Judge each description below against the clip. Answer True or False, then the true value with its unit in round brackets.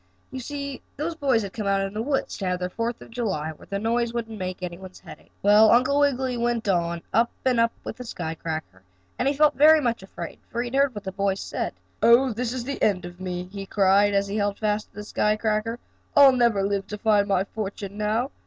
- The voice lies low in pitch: False (215 Hz)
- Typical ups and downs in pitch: True (3.8 semitones)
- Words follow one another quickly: True (245 wpm)